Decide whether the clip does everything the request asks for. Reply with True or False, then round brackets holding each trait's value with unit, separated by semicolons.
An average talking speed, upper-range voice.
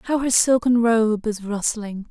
True (170 wpm; 225 Hz)